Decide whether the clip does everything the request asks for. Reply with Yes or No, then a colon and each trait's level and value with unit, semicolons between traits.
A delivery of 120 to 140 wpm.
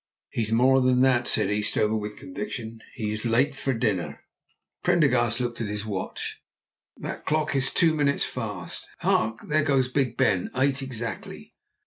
No: average, 160 wpm